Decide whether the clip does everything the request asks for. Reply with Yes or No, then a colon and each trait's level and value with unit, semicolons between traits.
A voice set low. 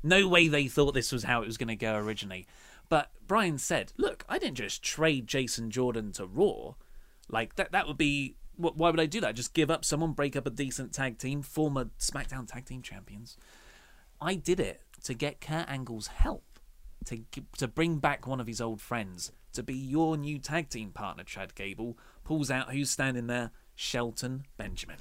Yes: low, 130 Hz